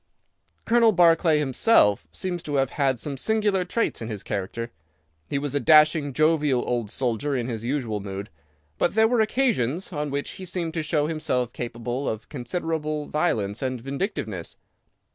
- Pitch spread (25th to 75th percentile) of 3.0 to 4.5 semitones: No, wide, 5.6 semitones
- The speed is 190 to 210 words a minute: No, average, 160 wpm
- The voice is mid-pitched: Yes, medium, 145 Hz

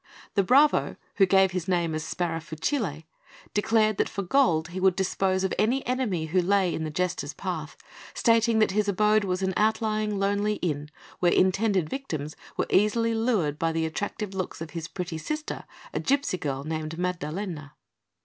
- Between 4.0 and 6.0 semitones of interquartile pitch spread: Yes, average, 4.7 semitones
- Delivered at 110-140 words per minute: No, average, 170 wpm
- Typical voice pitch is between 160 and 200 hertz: Yes, high, 190 Hz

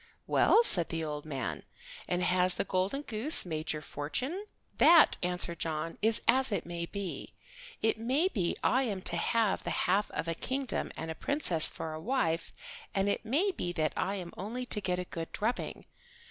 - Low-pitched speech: No, high, 190 Hz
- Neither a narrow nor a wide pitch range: No, wide, 6.7 semitones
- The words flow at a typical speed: Yes, average, 190 wpm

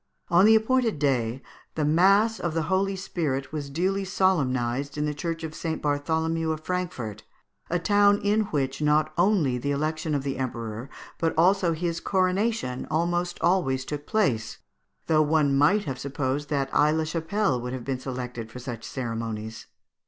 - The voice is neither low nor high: Yes, medium, 155 Hz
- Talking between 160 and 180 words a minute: Yes, average, 165 wpm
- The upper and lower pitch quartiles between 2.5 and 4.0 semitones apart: No, average, 5.3 semitones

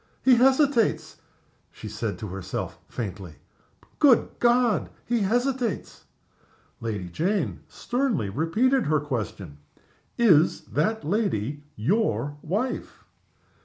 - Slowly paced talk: Yes, slow, 95 wpm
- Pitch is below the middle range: No, high, 190 Hz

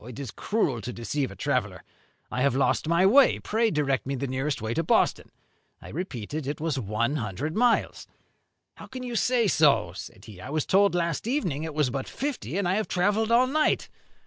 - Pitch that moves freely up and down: Yes, wide, 8.1 semitones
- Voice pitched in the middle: Yes, medium, 150 Hz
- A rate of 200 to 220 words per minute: Yes, fast, 205 wpm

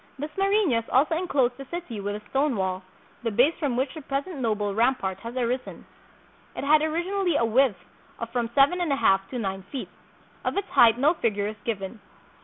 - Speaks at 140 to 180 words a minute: No, average, 195 wpm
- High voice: Yes, very high, 255 Hz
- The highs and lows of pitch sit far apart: Yes, wide, 5.7 semitones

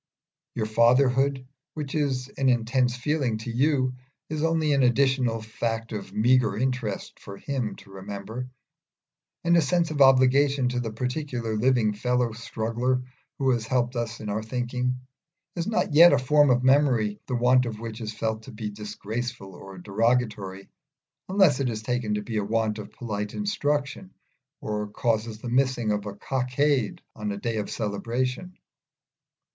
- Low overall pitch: Yes, low, 120 Hz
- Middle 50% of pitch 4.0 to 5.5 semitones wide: No, average, 3.5 semitones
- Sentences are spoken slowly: No, average, 160 wpm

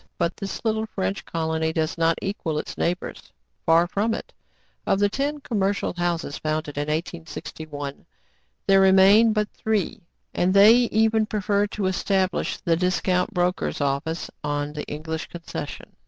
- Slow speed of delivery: No, average, 145 wpm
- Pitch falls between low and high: Yes, medium, 180 Hz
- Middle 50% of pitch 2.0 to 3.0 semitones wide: No, average, 4.3 semitones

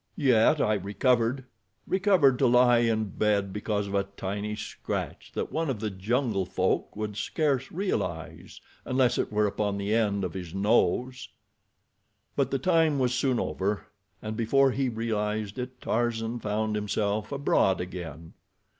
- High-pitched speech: No, low, 110 Hz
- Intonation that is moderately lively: Yes, average, 3.9 semitones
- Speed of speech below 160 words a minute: Yes, average, 145 wpm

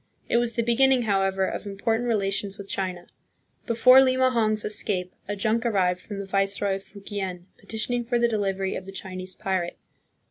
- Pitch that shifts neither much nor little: Yes, average, 3.2 semitones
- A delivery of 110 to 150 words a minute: No, average, 170 wpm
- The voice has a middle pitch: No, high, 200 Hz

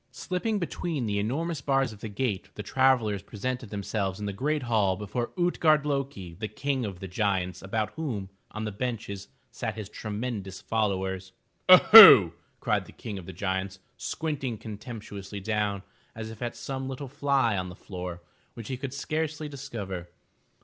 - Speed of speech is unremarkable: Yes, average, 165 wpm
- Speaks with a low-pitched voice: Yes, low, 110 Hz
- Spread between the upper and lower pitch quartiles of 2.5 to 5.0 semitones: No, wide, 5.5 semitones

